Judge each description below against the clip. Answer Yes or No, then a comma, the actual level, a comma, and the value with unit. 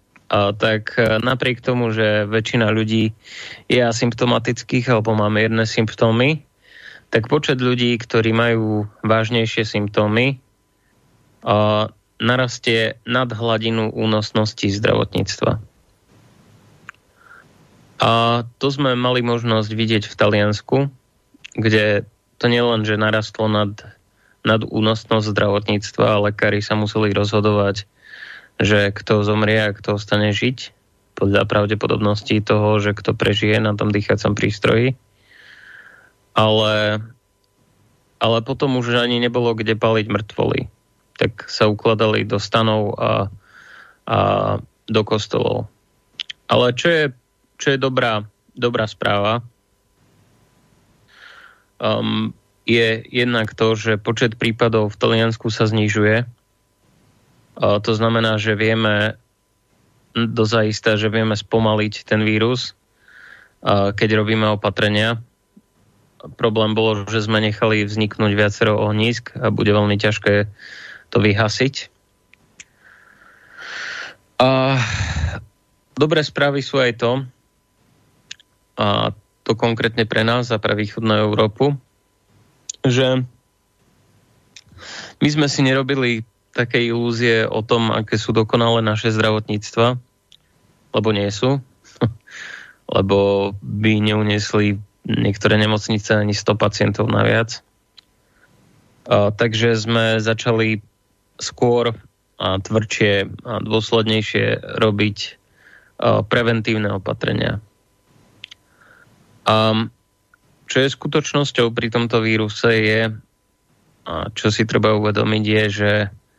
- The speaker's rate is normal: No, slow, 100 wpm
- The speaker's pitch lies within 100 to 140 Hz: Yes, low, 110 Hz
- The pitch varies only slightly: Yes, narrow, 2.0 semitones